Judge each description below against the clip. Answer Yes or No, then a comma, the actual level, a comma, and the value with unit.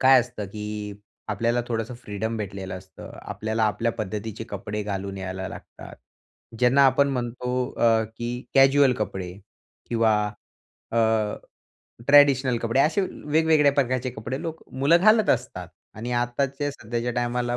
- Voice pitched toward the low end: Yes, low, 120 Hz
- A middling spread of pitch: Yes, average, 3.7 semitones